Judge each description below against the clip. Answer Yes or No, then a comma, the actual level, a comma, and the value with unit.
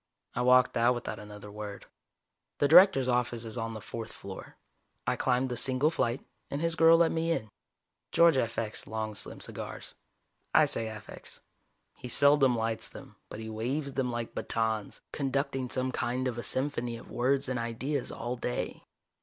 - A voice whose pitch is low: Yes, low, 125 Hz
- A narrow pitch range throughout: No, average, 3.4 semitones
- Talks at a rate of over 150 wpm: Yes, average, 170 wpm